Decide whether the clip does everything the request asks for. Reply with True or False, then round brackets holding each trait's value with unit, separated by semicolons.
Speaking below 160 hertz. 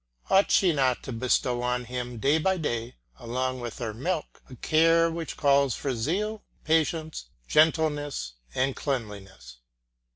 True (135 Hz)